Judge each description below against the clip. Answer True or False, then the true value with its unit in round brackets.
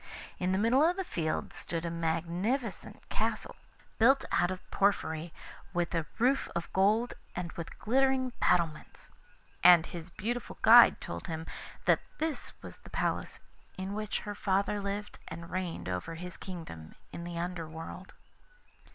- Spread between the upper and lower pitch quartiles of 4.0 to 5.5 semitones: True (4.4 semitones)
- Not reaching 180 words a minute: True (150 wpm)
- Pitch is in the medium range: True (180 Hz)